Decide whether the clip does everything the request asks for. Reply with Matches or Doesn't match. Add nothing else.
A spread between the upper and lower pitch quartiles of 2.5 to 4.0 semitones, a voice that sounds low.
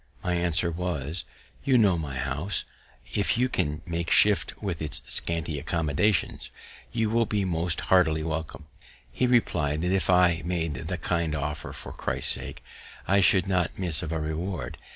Matches